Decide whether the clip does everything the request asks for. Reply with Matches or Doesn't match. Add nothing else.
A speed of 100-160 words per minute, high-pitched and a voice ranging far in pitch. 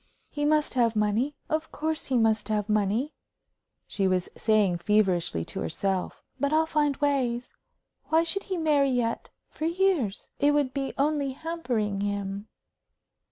Matches